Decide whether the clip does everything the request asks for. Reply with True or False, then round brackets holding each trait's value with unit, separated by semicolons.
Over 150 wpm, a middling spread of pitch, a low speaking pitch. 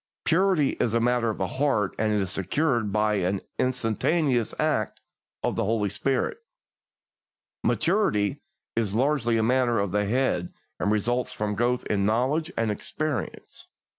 False (145 wpm; 4.2 semitones; 115 Hz)